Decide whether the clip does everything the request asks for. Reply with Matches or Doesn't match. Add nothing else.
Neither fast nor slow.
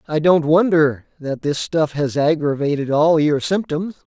Matches